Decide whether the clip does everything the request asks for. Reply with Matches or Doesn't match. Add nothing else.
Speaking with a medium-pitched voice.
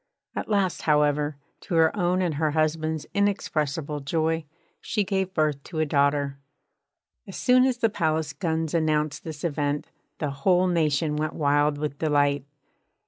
Matches